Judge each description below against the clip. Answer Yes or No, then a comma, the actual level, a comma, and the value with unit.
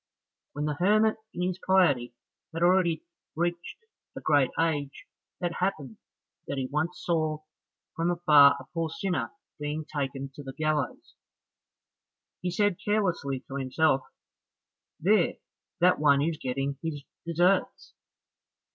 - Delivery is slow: Yes, slow, 130 wpm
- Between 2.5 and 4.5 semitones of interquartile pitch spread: Yes, average, 3.9 semitones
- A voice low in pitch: No, medium, 160 Hz